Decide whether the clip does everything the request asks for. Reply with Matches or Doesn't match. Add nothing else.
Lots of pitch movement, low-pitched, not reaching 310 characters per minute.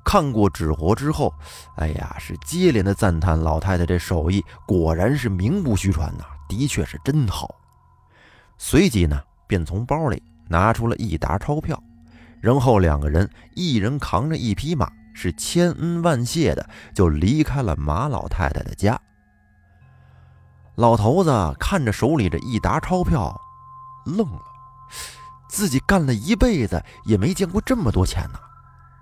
Matches